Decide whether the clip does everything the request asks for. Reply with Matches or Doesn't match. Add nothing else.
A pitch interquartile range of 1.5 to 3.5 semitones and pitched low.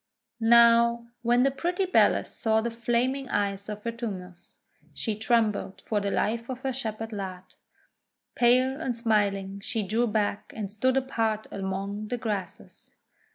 Doesn't match